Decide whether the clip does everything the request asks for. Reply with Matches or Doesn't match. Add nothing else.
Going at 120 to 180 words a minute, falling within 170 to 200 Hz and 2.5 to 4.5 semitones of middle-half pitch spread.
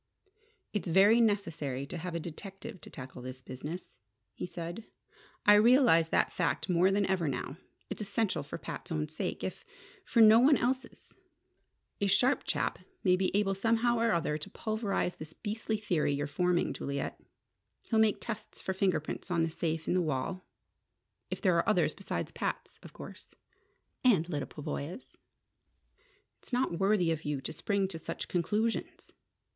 Doesn't match